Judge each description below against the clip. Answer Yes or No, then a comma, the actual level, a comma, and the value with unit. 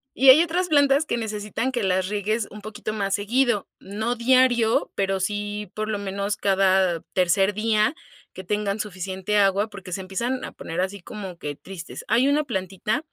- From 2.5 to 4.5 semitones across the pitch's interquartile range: Yes, average, 3.4 semitones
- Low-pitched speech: No, high, 205 Hz